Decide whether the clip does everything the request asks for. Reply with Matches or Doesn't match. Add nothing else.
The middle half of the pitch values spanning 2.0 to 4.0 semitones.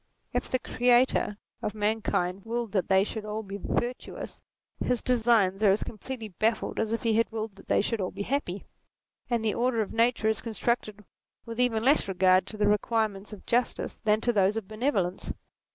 Matches